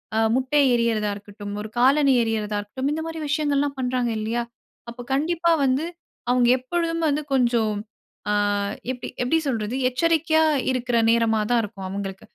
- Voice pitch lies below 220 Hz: No, very high, 250 Hz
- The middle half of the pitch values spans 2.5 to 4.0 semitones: No, average, 4.7 semitones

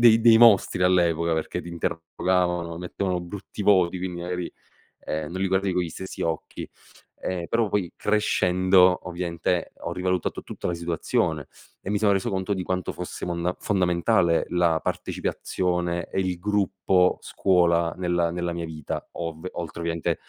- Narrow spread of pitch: Yes, narrow, 1.6 semitones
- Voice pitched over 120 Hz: No, very low, 90 Hz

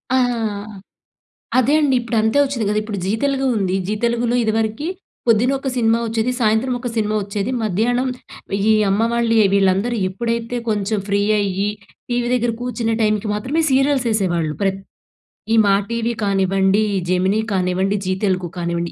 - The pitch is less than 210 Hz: No, high, 220 Hz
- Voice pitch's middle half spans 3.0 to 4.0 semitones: Yes, average, 3.5 semitones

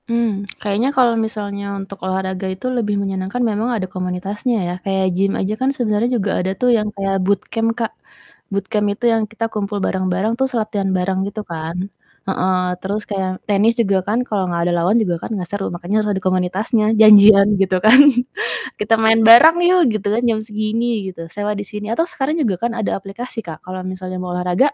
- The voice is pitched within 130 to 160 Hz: No, high, 205 Hz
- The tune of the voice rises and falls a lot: No, average, 2.8 semitones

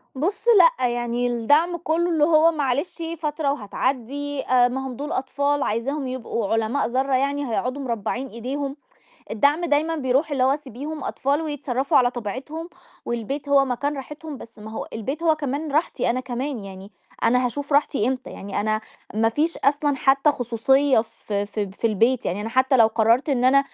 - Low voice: No, very high, 265 Hz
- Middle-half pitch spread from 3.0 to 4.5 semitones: Yes, average, 3.4 semitones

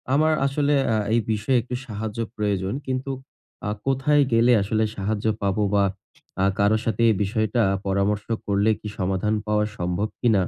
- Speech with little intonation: No, average, 3.4 semitones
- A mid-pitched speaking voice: No, low, 105 Hz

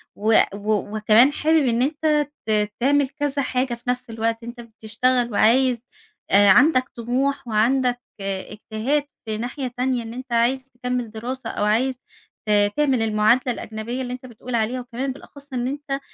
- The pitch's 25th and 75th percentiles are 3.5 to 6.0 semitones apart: No, average, 2.9 semitones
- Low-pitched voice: No, high, 245 Hz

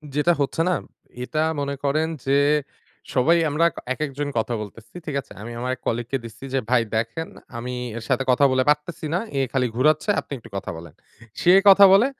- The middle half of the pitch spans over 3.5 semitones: Yes, average, 4.1 semitones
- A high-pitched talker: No, medium, 140 Hz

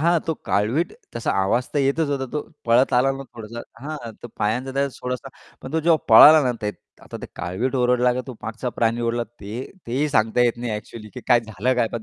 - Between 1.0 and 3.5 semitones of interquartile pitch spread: Yes, average, 2.9 semitones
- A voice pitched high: No, low, 125 Hz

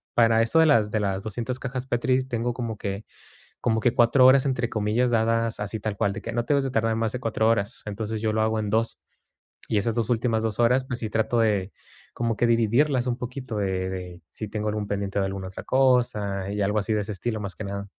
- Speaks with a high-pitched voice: No, low, 110 Hz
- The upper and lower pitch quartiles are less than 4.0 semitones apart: Yes, average, 2.8 semitones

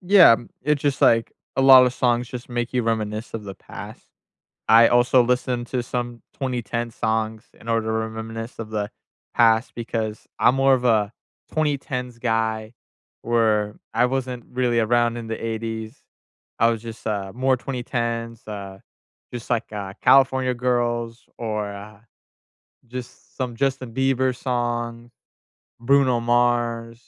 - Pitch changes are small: Yes, narrow, 2.0 semitones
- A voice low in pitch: Yes, low, 120 Hz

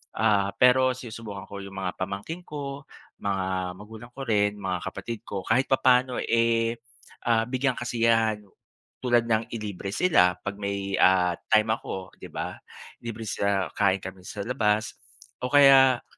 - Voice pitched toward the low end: Yes, low, 110 Hz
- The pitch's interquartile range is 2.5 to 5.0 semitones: Yes, average, 3.6 semitones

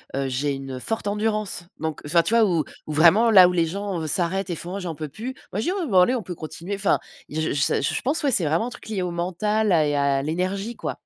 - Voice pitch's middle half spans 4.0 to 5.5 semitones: Yes, average, 5.1 semitones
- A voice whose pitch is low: No, medium, 180 Hz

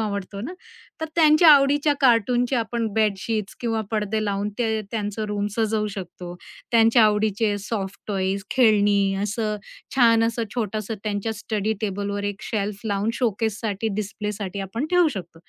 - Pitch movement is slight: Yes, narrow, 2.2 semitones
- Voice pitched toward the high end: Yes, high, 215 Hz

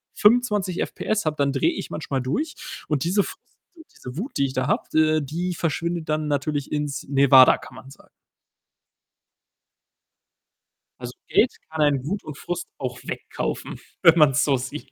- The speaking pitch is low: No, medium, 150 Hz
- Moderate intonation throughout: Yes, average, 3.9 semitones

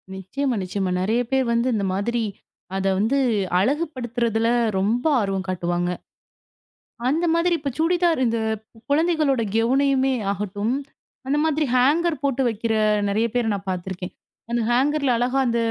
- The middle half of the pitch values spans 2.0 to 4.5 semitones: No, wide, 5.5 semitones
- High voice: Yes, high, 240 Hz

